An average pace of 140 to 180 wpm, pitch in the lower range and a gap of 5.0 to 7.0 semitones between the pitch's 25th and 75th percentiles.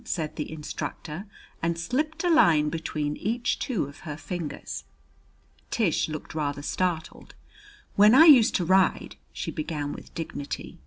No: average, 150 wpm; medium, 165 Hz; wide, 5.6 semitones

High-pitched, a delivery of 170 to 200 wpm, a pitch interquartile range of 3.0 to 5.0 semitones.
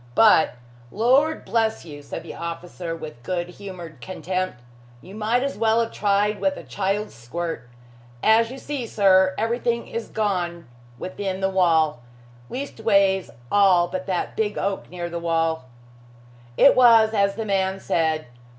No: high, 195 Hz; average, 150 wpm; average, 4.3 semitones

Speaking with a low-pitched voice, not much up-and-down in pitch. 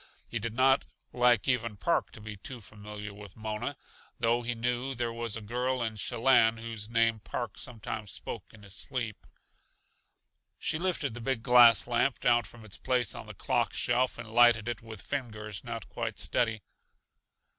Yes: low, 115 Hz; narrow, 2.1 semitones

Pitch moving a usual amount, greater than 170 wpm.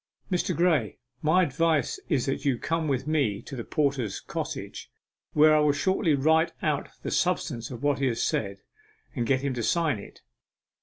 Yes: average, 4.1 semitones; average, 185 wpm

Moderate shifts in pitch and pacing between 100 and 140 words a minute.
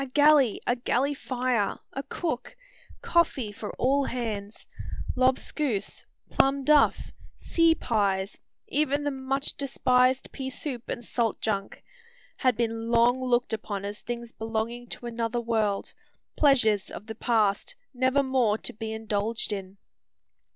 Yes: average, 3.3 semitones; slow, 135 wpm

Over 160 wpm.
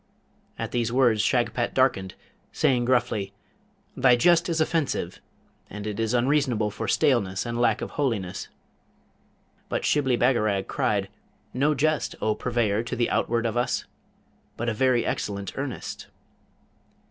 No: slow, 135 wpm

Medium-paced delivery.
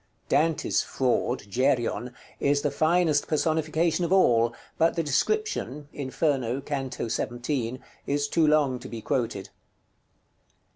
No: slow, 115 wpm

